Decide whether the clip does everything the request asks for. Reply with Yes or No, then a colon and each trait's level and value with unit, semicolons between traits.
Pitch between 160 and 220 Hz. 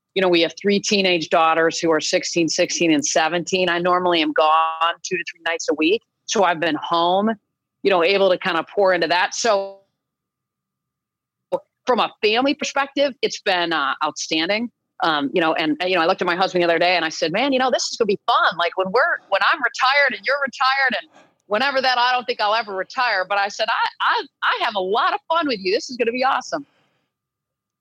Yes: high, 190 Hz